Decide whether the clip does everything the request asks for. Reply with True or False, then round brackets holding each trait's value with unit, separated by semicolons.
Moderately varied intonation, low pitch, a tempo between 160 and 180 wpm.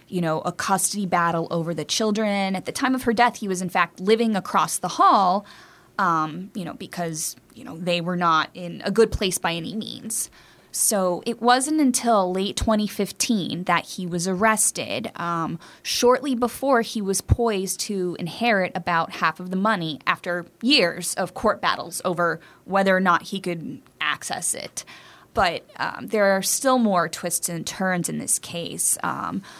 False (4.3 semitones; 190 Hz; 175 wpm)